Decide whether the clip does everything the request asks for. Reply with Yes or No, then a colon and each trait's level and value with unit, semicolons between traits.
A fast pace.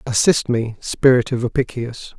No: slow, 135 wpm